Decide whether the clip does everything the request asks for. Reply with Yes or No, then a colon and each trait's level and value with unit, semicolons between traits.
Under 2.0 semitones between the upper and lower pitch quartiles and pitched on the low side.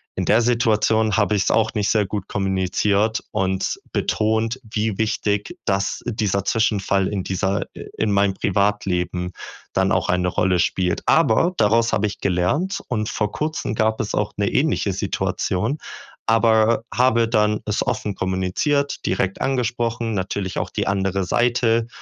No: average, 2.7 semitones; low, 105 Hz